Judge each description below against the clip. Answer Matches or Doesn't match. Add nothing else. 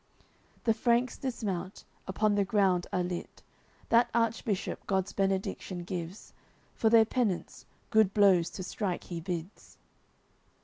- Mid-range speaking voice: Doesn't match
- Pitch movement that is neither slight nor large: Matches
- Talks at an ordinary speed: Doesn't match